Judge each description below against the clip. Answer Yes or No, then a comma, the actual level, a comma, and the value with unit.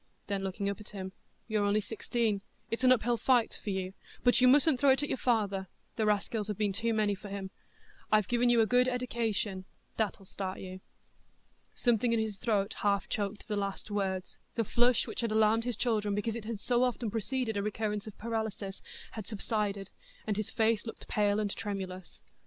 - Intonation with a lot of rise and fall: No, narrow, 2.6 semitones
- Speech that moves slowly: No, average, 200 wpm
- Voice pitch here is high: Yes, high, 215 Hz